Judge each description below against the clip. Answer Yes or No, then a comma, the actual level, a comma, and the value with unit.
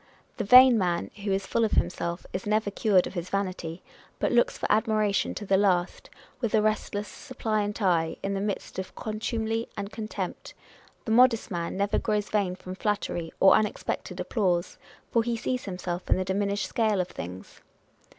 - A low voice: No, high, 205 Hz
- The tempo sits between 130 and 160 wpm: No, average, 180 wpm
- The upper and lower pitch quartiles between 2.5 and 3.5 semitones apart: Yes, average, 2.9 semitones